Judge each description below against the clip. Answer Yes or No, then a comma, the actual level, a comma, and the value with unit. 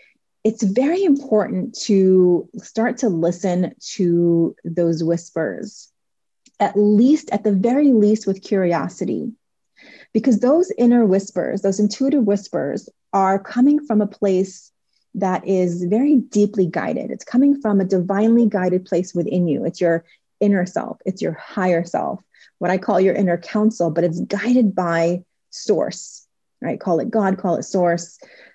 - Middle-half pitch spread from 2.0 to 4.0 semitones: No, average, 4.5 semitones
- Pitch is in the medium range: No, high, 200 Hz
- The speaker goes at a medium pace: Yes, average, 145 wpm